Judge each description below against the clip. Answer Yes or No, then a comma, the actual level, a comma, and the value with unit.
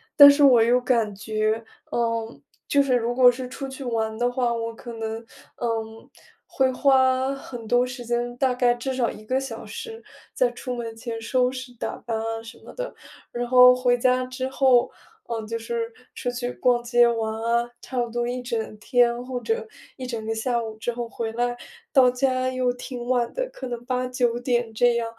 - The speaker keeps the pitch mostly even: Yes, narrow, 1.8 semitones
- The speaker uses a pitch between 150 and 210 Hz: No, high, 245 Hz